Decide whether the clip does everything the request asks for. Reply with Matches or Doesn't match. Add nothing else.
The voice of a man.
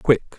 Matches